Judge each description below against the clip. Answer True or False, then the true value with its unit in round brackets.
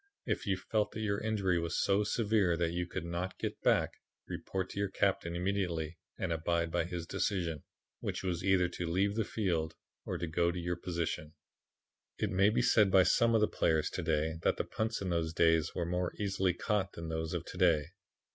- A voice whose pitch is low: True (90 Hz)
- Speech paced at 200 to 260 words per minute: True (205 wpm)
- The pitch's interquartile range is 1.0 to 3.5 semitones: True (3.0 semitones)